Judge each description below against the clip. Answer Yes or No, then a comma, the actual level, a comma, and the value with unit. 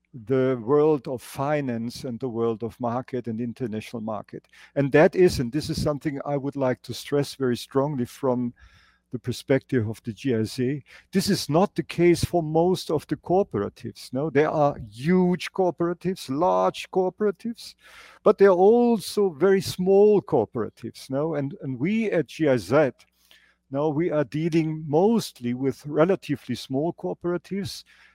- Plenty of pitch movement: Yes, wide, 5.7 semitones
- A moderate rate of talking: Yes, average, 150 wpm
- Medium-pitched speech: Yes, medium, 145 Hz